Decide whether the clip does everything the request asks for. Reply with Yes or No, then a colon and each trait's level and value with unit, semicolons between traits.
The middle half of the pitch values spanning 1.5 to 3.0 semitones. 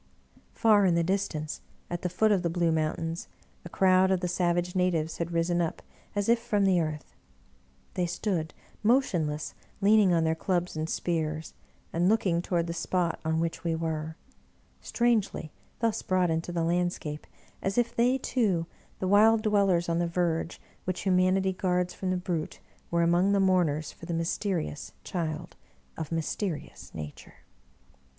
Yes: average, 2.7 semitones